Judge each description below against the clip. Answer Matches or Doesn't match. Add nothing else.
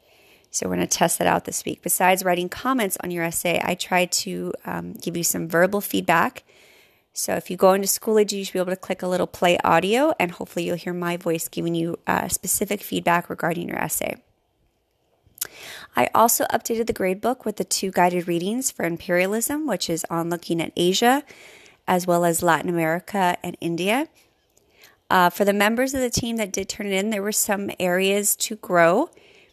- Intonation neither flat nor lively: Matches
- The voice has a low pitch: Doesn't match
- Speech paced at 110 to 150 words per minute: Doesn't match